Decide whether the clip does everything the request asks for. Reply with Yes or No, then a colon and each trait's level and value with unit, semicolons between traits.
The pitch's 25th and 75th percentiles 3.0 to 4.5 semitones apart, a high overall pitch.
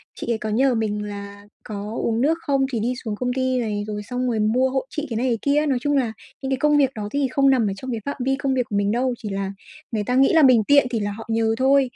Yes: average, 3.8 semitones; high, 245 Hz